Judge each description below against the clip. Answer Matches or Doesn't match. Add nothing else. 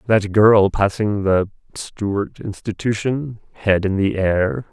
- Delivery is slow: Matches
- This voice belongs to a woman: Doesn't match